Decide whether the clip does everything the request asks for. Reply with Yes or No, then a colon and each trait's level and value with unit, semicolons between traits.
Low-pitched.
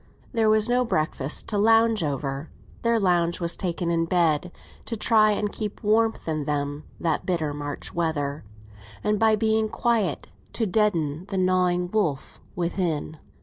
No: medium, 180 Hz